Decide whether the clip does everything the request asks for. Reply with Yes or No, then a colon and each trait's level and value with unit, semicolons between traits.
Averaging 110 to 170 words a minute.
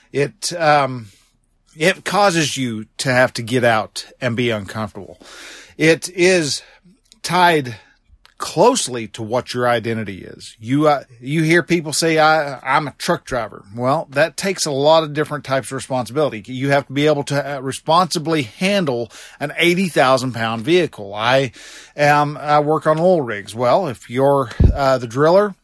Yes: average, 160 wpm